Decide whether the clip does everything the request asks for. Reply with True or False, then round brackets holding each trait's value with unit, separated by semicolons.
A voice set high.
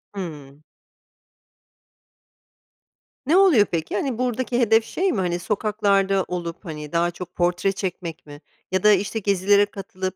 True (195 Hz)